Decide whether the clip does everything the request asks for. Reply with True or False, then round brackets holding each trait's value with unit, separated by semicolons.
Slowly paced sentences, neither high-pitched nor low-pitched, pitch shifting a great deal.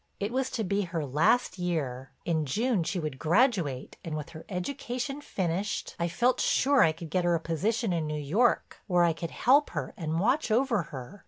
False (200 wpm; 175 Hz; 6.7 semitones)